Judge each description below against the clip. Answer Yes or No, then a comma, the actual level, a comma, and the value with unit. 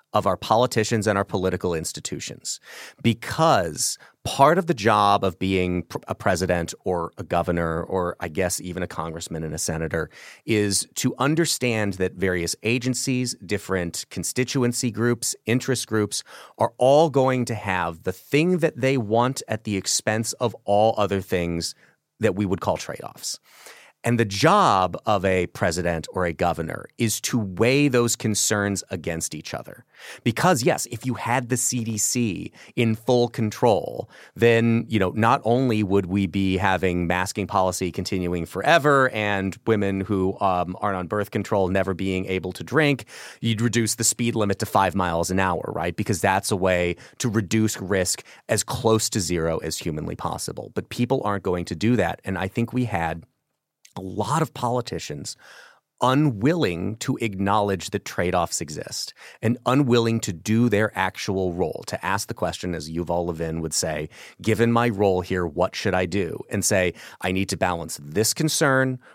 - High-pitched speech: No, low, 105 Hz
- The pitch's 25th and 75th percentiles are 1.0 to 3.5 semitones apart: No, average, 4.4 semitones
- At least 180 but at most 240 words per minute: No, average, 170 wpm